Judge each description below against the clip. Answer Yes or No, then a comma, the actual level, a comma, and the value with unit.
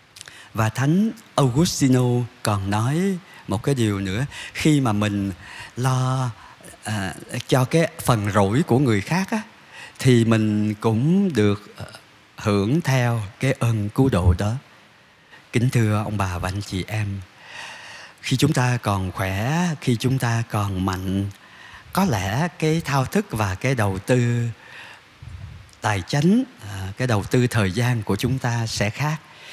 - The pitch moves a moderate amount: Yes, average, 4.5 semitones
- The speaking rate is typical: No, slow, 145 wpm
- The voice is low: Yes, low, 120 Hz